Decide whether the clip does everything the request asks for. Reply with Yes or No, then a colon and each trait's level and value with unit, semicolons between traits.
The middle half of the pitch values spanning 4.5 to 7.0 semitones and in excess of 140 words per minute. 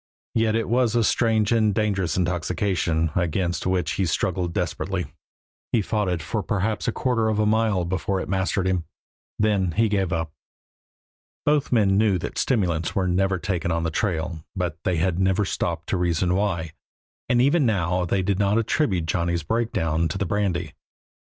No: average, 3.7 semitones; average, 175 wpm